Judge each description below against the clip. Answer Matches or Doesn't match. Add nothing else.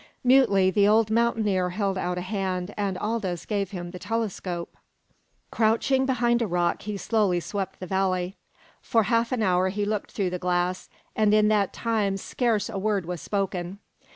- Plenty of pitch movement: Doesn't match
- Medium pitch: Doesn't match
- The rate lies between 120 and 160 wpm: Doesn't match